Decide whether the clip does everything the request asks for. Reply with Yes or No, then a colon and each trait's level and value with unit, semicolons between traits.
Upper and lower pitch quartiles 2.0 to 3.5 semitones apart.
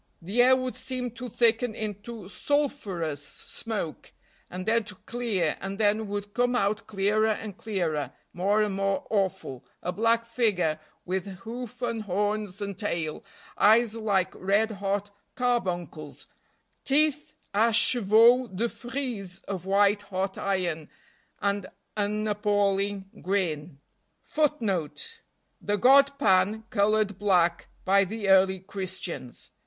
Yes: average, 3.2 semitones